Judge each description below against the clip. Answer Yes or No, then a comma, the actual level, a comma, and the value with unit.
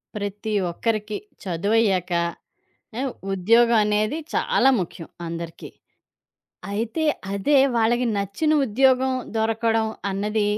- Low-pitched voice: No, high, 215 Hz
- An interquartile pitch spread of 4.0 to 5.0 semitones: No, average, 2.8 semitones